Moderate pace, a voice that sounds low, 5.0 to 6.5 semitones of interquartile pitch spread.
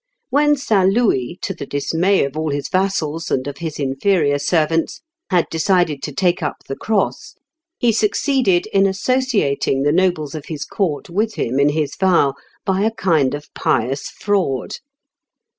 No: average, 160 wpm; medium, 170 Hz; wide, 5.5 semitones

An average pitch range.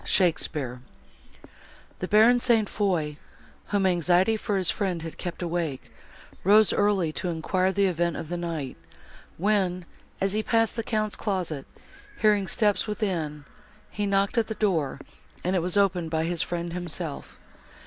Yes: average, 3.7 semitones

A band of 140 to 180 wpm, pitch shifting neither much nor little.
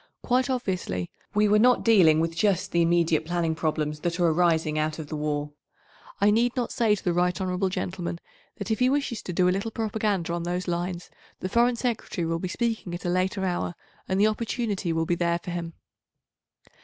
No: fast, 205 wpm; average, 4.0 semitones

